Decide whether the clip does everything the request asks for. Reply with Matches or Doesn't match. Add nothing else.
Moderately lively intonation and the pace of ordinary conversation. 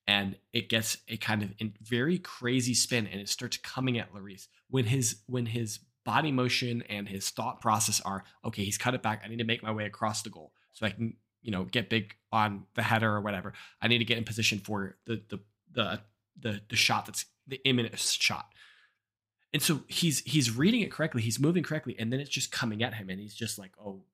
Doesn't match